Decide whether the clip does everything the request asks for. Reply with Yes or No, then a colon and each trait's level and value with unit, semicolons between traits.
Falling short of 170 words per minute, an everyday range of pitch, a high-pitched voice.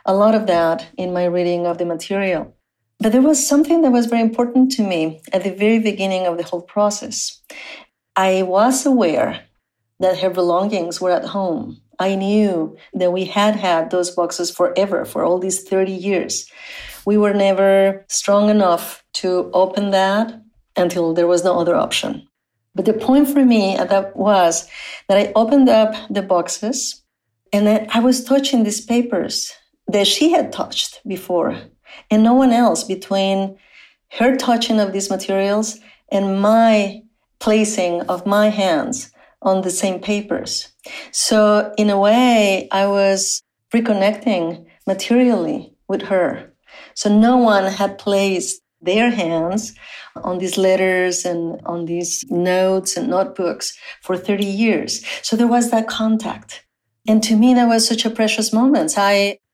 Yes: average, 155 wpm; average, 3.3 semitones; high, 200 Hz